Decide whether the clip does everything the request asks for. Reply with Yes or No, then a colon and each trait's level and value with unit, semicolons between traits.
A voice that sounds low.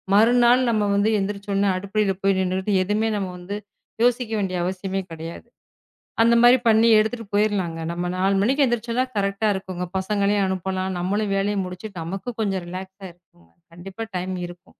No: high, 195 Hz